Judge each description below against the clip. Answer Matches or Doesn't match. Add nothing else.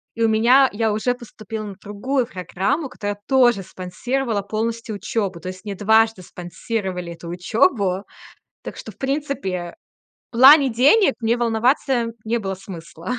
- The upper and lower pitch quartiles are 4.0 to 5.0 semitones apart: Matches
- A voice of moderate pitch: Doesn't match